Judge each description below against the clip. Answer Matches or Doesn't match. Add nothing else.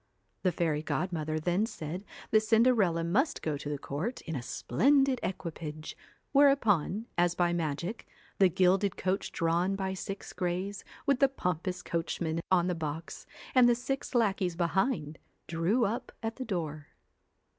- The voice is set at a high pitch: Doesn't match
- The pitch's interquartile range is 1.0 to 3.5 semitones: Doesn't match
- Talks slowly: Doesn't match